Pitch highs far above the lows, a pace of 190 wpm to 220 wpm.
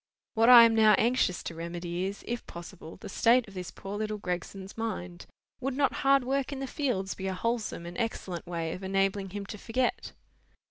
No: average, 4.7 semitones; average, 200 wpm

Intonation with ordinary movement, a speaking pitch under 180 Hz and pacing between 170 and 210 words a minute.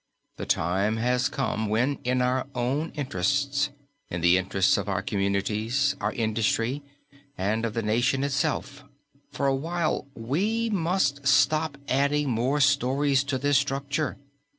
No: average, 4.3 semitones; low, 135 Hz; average, 140 wpm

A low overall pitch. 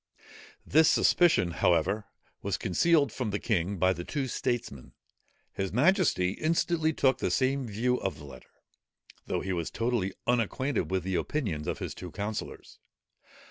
Yes: low, 110 Hz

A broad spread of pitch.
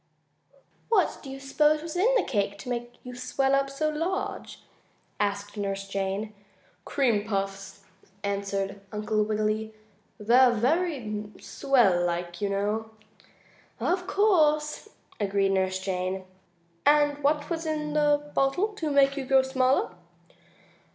Yes: wide, 6.7 semitones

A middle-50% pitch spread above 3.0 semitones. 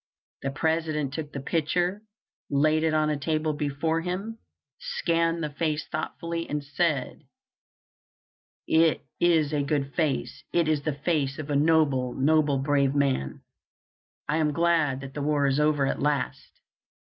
No: narrow, 2.4 semitones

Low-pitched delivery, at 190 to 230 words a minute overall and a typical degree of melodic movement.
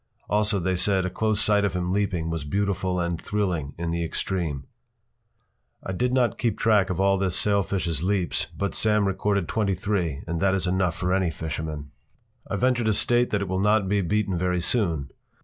Yes: very low, 95 Hz; average, 195 wpm; average, 3.1 semitones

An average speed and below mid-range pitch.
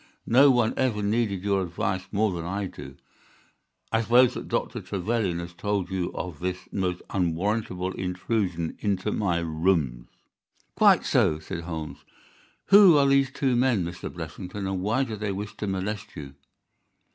Yes: average, 155 wpm; very low, 95 Hz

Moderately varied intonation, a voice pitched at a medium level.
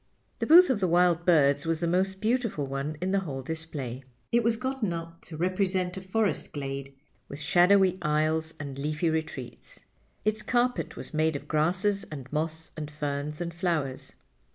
Yes: average, 4.1 semitones; medium, 165 Hz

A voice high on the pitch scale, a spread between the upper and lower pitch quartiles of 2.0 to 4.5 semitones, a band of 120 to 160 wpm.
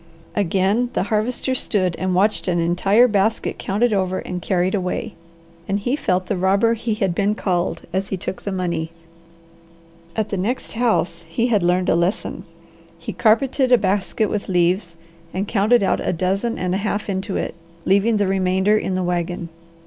No: high, 195 Hz; average, 2.9 semitones; average, 180 wpm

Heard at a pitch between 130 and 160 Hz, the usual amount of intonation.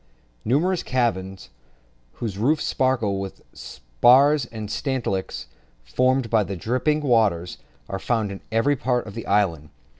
No: low, 115 Hz; average, 4.9 semitones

